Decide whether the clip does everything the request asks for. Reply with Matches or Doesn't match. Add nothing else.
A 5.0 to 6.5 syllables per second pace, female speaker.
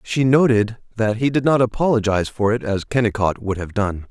Doesn't match